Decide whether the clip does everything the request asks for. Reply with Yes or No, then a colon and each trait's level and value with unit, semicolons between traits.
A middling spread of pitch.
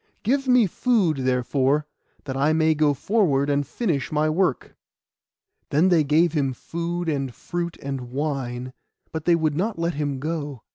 Yes: average, 3.7 semitones